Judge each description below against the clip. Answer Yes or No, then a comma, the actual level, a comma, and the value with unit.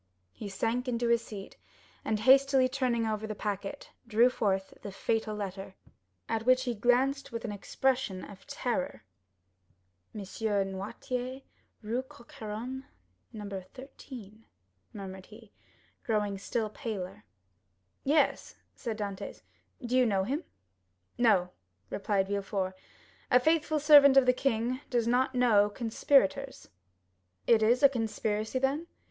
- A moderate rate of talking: No, slow, 130 wpm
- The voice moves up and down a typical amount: Yes, average, 3.9 semitones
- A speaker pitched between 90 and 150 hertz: No, high, 230 Hz